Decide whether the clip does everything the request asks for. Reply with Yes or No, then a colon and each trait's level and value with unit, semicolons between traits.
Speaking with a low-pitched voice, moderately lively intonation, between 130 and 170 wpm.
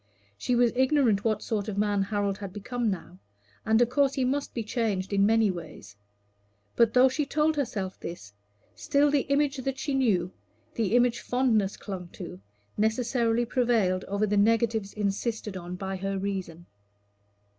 No: high, 220 Hz; average, 4.2 semitones; average, 165 wpm